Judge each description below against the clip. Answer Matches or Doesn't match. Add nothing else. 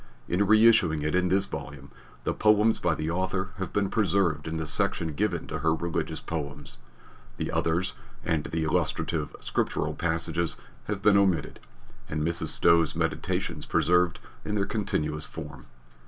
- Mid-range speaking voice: Doesn't match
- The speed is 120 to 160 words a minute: Matches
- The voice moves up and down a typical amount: Matches